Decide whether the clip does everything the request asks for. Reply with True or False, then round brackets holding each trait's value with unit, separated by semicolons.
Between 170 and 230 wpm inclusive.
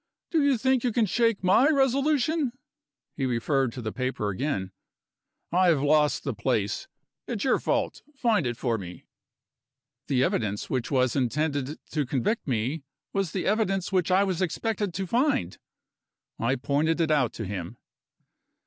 False (160 wpm)